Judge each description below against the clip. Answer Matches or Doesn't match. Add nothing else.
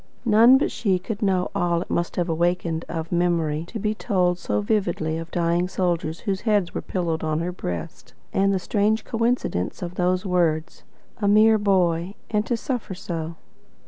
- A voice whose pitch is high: Doesn't match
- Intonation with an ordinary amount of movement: Matches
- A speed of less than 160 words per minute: Doesn't match